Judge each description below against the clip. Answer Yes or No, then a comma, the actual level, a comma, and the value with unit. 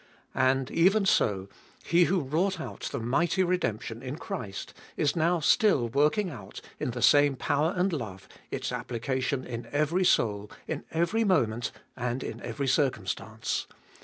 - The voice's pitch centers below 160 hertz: Yes, medium, 140 Hz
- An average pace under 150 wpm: No, average, 155 wpm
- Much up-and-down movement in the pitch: Yes, wide, 6.7 semitones